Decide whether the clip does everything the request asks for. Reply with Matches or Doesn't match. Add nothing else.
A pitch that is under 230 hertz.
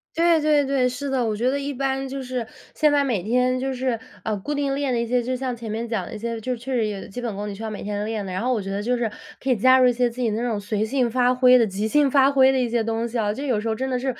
Doesn't match